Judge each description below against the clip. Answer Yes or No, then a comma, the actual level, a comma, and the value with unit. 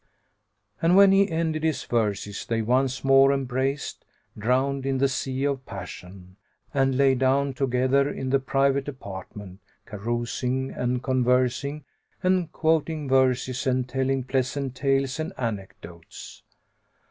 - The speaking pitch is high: No, low, 130 Hz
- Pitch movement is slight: Yes, narrow, 1.9 semitones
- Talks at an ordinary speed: No, slow, 125 wpm